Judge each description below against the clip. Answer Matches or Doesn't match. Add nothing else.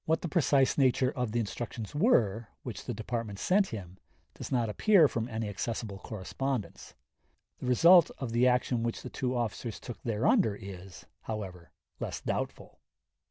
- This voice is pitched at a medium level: Doesn't match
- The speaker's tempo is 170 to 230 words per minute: Doesn't match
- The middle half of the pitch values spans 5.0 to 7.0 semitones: Doesn't match